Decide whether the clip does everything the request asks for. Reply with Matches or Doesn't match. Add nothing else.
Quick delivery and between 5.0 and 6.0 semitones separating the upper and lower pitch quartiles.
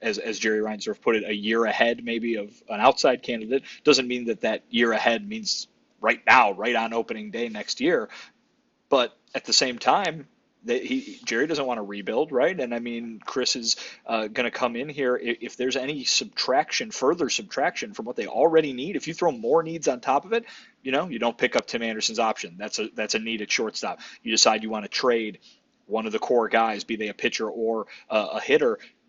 Matches